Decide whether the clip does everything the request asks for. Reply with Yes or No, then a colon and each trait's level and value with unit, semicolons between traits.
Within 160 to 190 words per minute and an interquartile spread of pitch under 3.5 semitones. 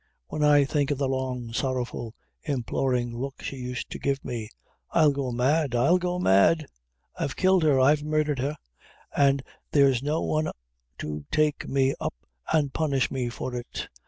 Yes: average, 165 wpm; average, 3.0 semitones